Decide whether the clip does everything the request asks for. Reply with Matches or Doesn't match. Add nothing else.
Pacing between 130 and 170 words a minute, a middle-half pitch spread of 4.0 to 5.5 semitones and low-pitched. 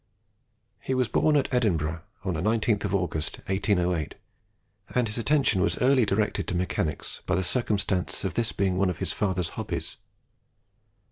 Matches